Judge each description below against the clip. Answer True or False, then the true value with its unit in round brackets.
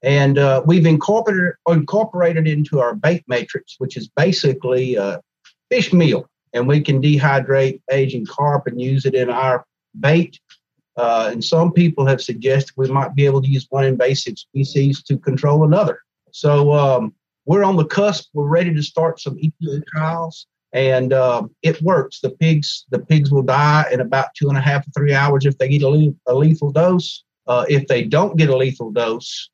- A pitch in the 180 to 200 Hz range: False (140 Hz)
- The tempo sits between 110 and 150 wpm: False (190 wpm)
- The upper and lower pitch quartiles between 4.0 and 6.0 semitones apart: False (3.3 semitones)